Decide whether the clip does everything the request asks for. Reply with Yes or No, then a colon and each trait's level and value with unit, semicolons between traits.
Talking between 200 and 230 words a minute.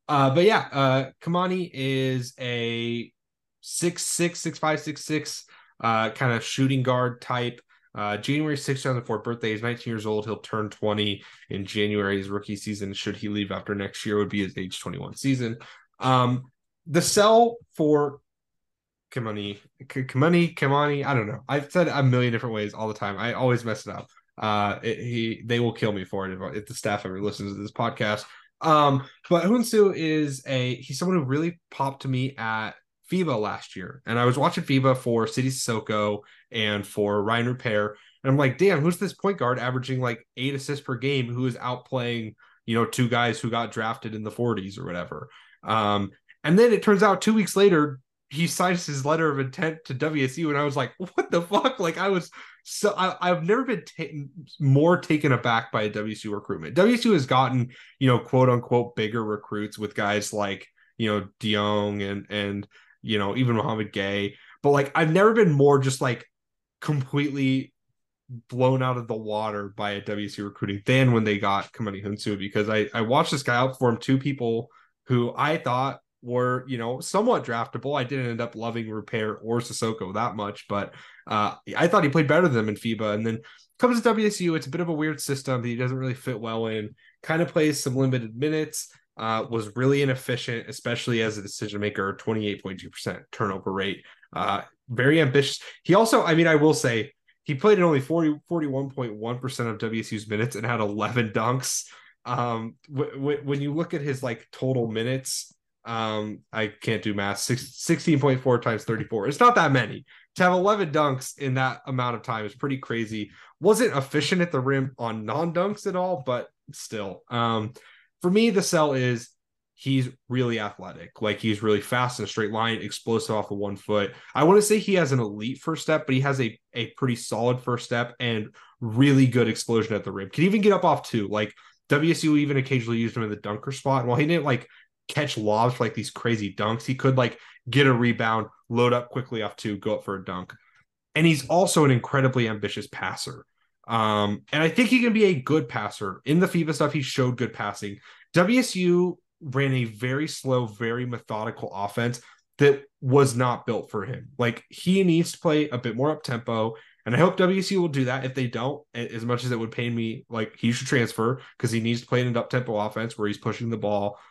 Yes: fast, 205 wpm